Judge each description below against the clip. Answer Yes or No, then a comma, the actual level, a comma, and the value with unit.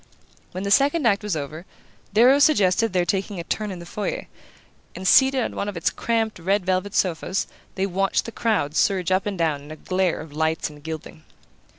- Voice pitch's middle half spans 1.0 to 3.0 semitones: No, average, 4.1 semitones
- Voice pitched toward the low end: No, high, 190 Hz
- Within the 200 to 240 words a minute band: Yes, fast, 205 wpm